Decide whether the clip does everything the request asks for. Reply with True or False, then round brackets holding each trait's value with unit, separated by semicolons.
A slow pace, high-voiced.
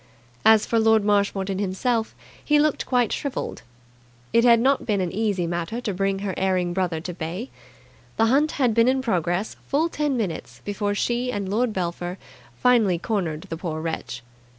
False (175 wpm; 205 Hz)